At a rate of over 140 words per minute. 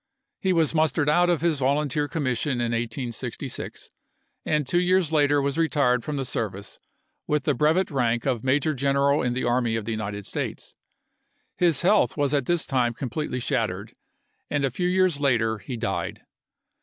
Yes: average, 170 wpm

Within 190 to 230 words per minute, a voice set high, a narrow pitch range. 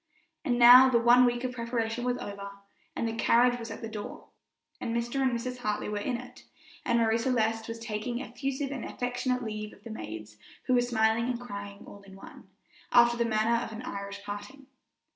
Yes: average, 200 wpm; high, 235 Hz; narrow, 2.3 semitones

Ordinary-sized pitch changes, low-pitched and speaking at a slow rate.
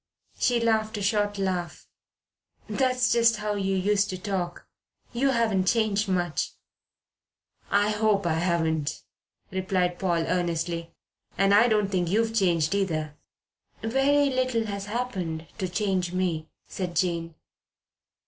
No: average, 3.8 semitones; high, 195 Hz; slow, 130 wpm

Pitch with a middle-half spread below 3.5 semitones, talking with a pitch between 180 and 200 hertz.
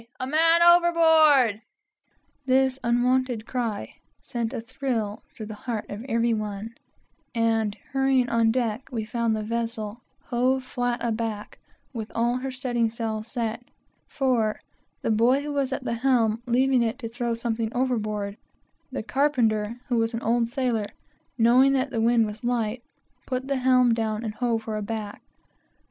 No: narrow, 2.6 semitones; high, 235 Hz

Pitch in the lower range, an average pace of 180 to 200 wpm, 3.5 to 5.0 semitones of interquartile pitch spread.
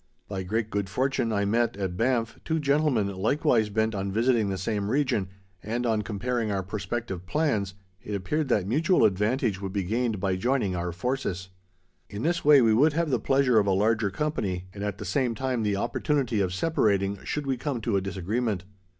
Yes: low, 110 Hz; average, 195 wpm; average, 4.6 semitones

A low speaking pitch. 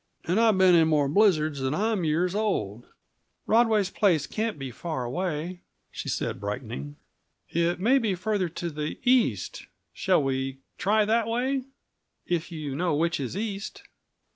No: medium, 175 Hz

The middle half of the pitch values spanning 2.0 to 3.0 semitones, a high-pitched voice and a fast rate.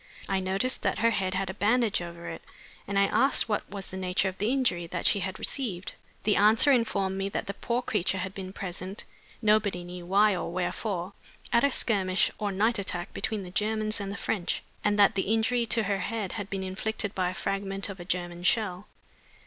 Yes: narrow, 2.6 semitones; high, 195 Hz; fast, 215 wpm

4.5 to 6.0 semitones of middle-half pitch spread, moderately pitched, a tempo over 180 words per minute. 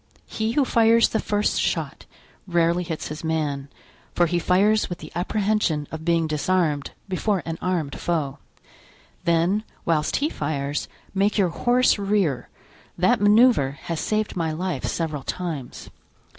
No: average, 5.0 semitones; medium, 175 Hz; average, 145 wpm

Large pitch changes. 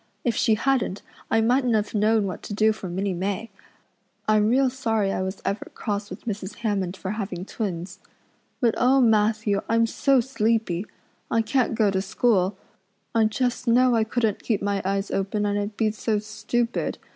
No: narrow, 2.5 semitones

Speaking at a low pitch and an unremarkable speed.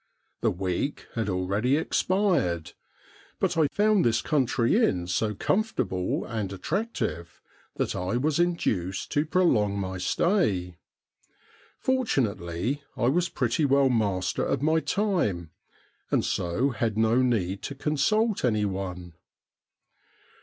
No: low, 115 Hz; slow, 120 wpm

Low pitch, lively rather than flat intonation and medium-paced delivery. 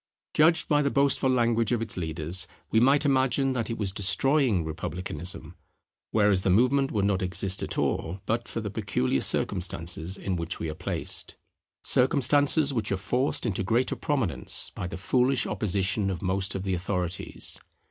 Yes: low, 100 Hz; wide, 5.7 semitones; average, 170 wpm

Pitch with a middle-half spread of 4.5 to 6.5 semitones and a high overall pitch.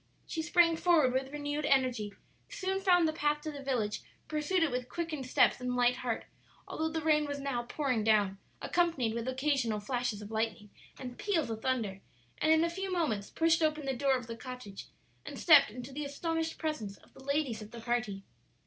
Yes: average, 5.0 semitones; very high, 270 Hz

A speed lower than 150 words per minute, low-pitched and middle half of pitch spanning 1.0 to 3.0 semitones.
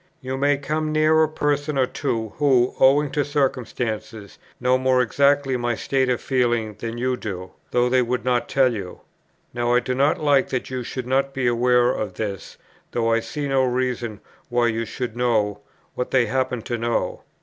No: average, 190 wpm; low, 125 Hz; narrow, 2.4 semitones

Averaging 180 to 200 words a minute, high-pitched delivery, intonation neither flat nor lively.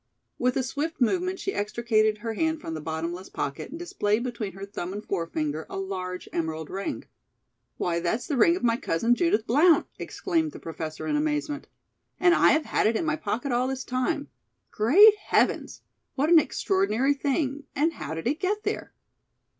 No: average, 185 wpm; high, 245 Hz; wide, 8.1 semitones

